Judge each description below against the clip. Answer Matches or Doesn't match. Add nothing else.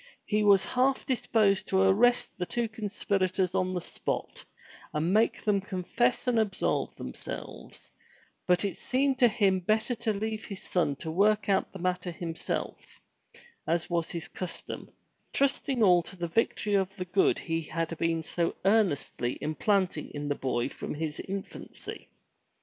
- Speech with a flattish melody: Doesn't match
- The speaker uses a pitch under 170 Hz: Doesn't match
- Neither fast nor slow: Matches